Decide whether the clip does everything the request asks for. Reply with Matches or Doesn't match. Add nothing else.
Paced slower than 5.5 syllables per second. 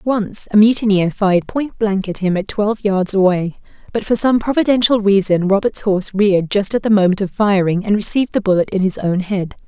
Doesn't match